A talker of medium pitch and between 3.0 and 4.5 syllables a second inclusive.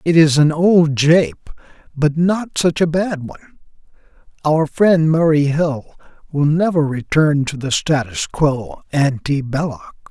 Yes: medium, 155 Hz; 3.8 syllables/s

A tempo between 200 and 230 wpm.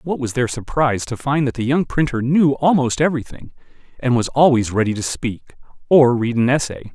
Yes: fast, 205 wpm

